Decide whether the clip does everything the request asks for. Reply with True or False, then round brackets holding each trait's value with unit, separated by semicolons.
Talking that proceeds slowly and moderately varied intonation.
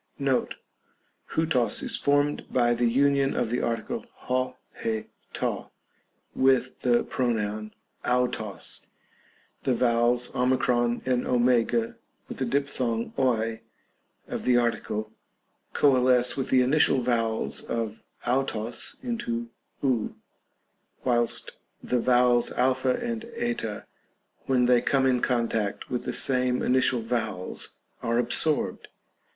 False (115 wpm; 2.0 semitones)